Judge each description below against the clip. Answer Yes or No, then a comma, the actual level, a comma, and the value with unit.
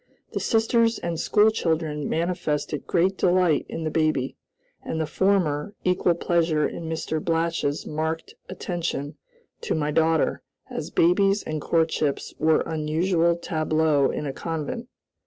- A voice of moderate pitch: Yes, medium, 165 Hz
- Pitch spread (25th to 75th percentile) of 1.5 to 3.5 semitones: Yes, narrow, 2.5 semitones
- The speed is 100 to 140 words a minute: Yes, slow, 135 wpm